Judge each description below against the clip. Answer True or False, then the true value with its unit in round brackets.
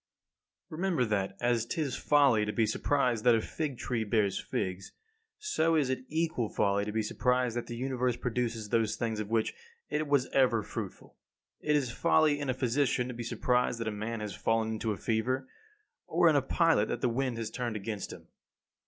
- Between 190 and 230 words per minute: True (200 wpm)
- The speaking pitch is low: True (120 Hz)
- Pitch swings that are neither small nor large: True (3.6 semitones)